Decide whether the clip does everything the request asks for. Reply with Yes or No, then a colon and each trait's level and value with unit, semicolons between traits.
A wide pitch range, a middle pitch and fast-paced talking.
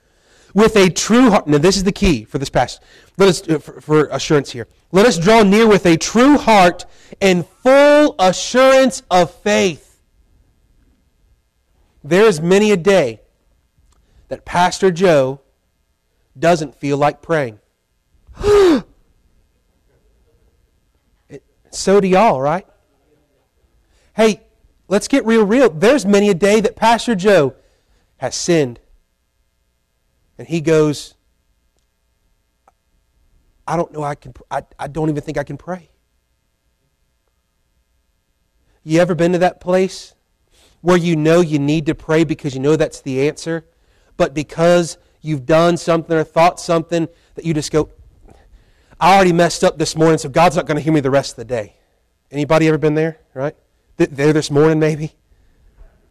No: wide, 5.8 semitones; medium, 160 Hz; average, 145 wpm